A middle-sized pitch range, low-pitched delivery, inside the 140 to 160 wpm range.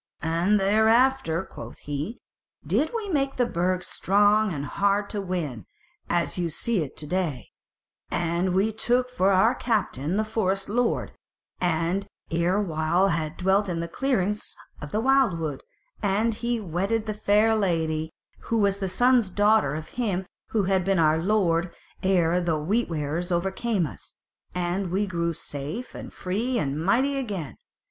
No: average, 4.4 semitones; high, 190 Hz; average, 155 wpm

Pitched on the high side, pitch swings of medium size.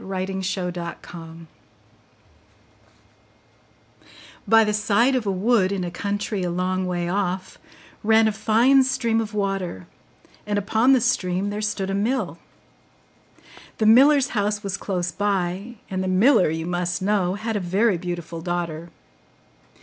Yes: high, 195 Hz; average, 3.3 semitones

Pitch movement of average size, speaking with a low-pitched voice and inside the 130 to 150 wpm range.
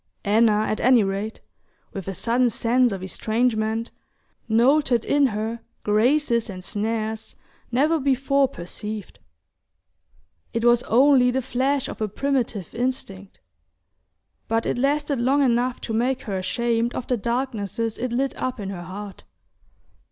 No: average, 3.2 semitones; high, 235 Hz; slow, 135 wpm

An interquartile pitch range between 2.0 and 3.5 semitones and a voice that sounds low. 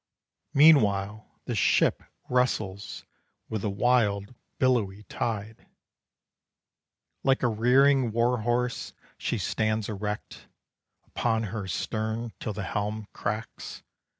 Yes: average, 2.9 semitones; low, 110 Hz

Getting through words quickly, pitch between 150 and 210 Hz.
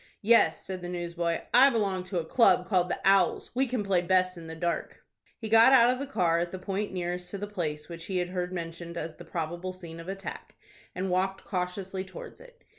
Yes: fast, 225 wpm; medium, 185 Hz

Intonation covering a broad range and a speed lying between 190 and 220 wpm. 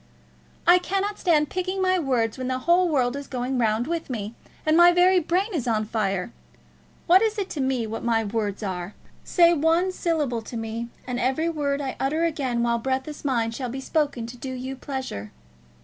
Yes: wide, 6.2 semitones; average, 200 wpm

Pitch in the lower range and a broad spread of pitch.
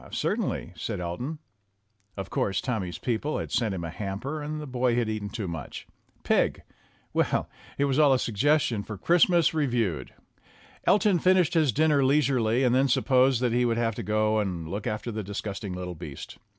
Yes: low, 120 Hz; wide, 5.7 semitones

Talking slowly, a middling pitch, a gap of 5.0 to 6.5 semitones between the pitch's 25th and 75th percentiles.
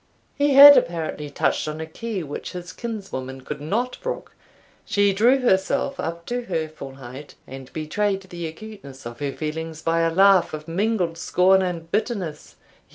No: average, 165 wpm; medium, 170 Hz; average, 5.3 semitones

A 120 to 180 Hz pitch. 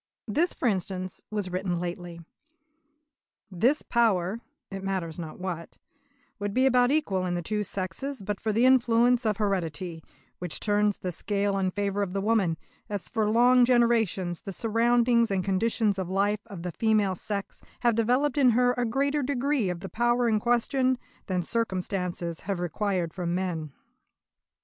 No: high, 205 Hz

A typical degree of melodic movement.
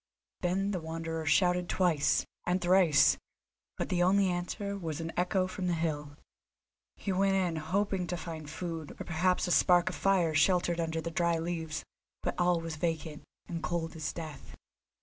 No: narrow, 2.1 semitones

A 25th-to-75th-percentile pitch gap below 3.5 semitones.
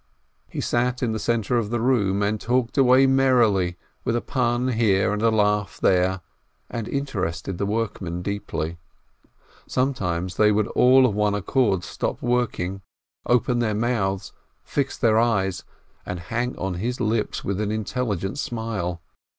No: average, 4.0 semitones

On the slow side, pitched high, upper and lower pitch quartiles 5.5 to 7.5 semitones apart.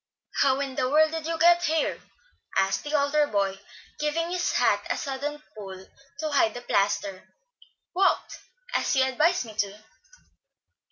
No: average, 155 wpm; very high, 280 Hz; wide, 6.6 semitones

